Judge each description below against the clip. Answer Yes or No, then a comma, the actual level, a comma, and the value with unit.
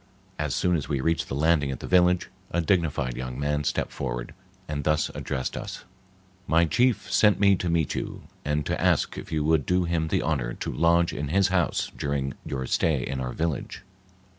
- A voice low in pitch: Yes, very low, 75 Hz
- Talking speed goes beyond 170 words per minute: Yes, average, 200 wpm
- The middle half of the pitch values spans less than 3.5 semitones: No, average, 3.8 semitones